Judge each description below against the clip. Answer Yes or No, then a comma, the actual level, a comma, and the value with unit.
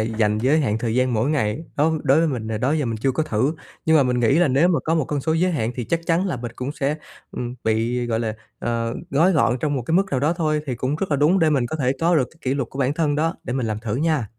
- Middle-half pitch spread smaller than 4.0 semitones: No, average, 4.8 semitones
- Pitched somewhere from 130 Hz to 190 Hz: Yes, low, 135 Hz